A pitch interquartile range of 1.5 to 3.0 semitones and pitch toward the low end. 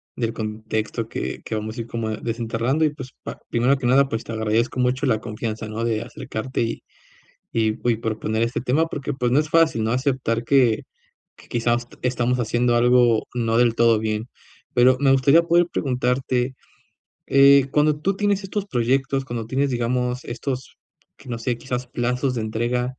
Yes: narrow, 2.6 semitones; low, 120 Hz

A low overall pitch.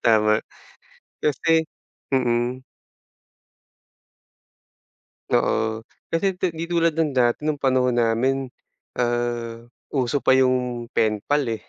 Yes: low, 125 Hz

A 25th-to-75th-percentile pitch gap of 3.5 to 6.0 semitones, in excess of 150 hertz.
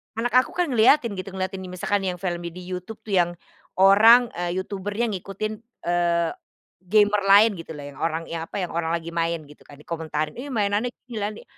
Yes: average, 4.0 semitones; high, 190 Hz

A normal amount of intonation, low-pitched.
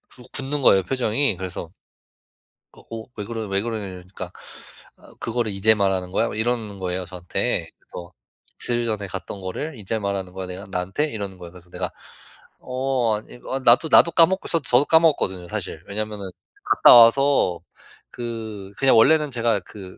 Yes: average, 4.6 semitones; low, 105 Hz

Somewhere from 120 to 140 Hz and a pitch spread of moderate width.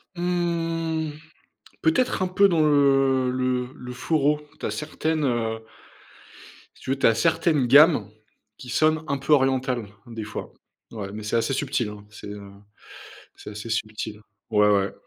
No: low, 135 Hz; wide, 5.8 semitones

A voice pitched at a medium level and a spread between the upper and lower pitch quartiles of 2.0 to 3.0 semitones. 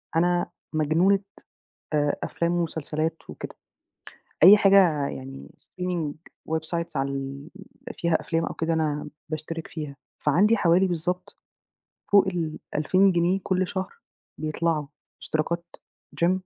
Yes: medium, 165 Hz; narrow, 2.6 semitones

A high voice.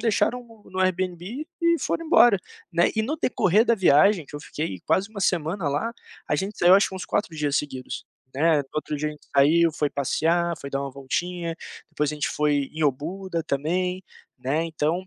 No: medium, 170 Hz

